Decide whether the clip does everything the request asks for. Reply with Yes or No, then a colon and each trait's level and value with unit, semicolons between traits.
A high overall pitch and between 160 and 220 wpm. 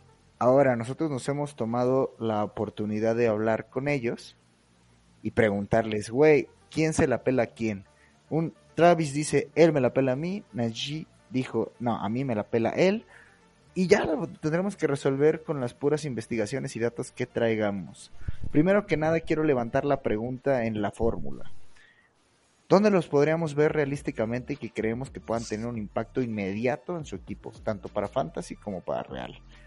No: low, 125 Hz; average, 170 wpm